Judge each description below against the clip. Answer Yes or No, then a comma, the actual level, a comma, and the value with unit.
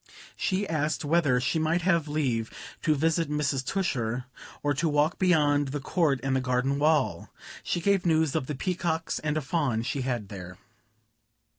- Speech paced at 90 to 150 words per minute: No, average, 170 wpm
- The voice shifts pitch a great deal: No, average, 3.6 semitones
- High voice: No, medium, 150 Hz